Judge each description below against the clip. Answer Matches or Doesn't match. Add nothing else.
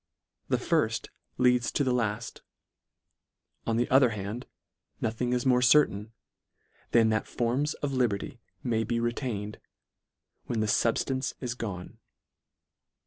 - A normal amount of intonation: Doesn't match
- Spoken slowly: Matches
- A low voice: Matches